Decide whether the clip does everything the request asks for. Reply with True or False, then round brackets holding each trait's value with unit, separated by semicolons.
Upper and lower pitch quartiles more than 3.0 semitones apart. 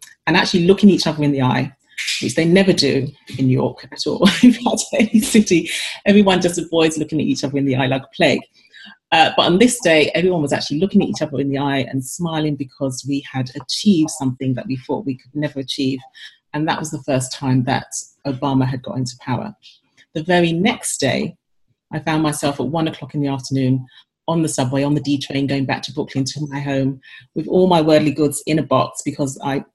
True (3.4 semitones)